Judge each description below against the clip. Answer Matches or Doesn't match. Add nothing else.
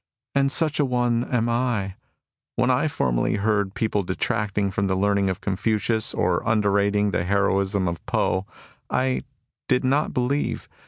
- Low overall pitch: Matches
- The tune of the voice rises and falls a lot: Doesn't match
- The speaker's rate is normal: Matches